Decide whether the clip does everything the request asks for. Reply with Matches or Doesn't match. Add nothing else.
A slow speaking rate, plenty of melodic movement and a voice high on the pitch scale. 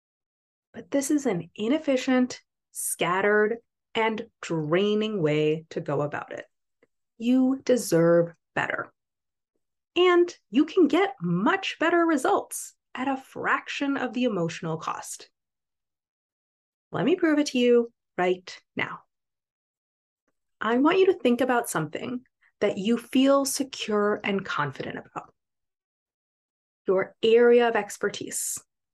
Matches